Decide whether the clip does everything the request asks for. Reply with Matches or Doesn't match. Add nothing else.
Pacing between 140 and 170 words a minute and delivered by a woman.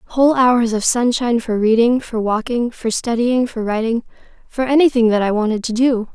Doesn't match